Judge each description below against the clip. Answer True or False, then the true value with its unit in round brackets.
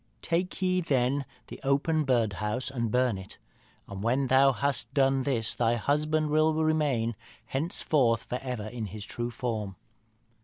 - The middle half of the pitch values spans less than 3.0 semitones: False (4.2 semitones)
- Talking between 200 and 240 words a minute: False (155 wpm)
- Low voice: True (130 Hz)